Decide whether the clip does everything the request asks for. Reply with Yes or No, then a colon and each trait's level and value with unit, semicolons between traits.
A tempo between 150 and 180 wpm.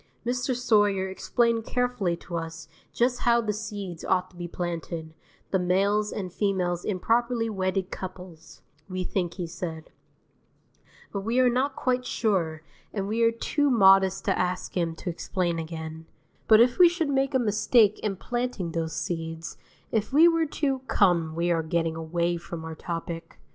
Yes: average, 170 wpm